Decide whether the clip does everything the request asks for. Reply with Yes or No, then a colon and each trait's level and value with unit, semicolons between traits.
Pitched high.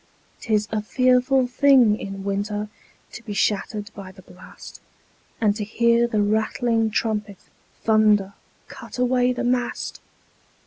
Yes: high, 220 Hz